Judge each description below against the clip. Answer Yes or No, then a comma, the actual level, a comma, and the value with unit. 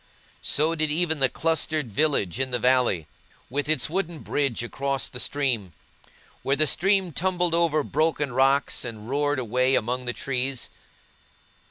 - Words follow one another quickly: No, average, 150 wpm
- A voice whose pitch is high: No, medium, 140 Hz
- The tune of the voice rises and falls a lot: No, average, 3.8 semitones